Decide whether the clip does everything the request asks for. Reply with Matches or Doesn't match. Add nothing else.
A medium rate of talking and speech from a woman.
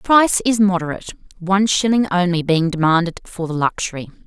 Matches